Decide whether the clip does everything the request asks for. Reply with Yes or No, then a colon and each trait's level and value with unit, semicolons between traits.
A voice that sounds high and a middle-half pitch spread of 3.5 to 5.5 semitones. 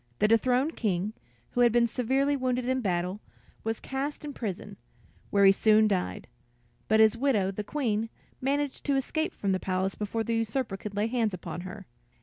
Yes: high, 225 Hz; average, 4.4 semitones